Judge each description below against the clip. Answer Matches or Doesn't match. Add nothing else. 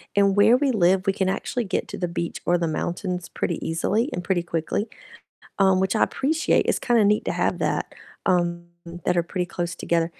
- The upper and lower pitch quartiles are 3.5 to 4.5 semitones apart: Doesn't match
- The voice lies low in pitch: Doesn't match